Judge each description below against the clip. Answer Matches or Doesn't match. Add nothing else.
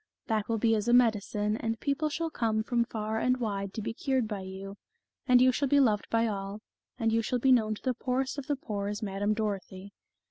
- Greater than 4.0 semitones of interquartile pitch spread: Doesn't match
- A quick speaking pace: Matches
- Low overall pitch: Doesn't match